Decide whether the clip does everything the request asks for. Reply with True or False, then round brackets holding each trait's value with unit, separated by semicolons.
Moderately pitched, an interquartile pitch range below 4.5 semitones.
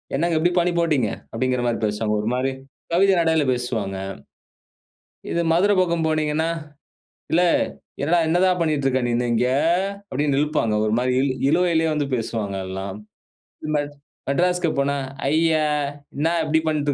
False (150 Hz; 4.9 semitones)